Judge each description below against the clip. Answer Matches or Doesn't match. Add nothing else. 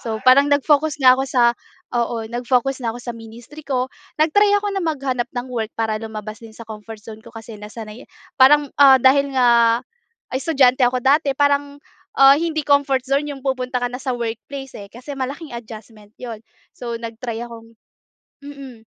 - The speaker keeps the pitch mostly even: Doesn't match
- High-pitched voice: Matches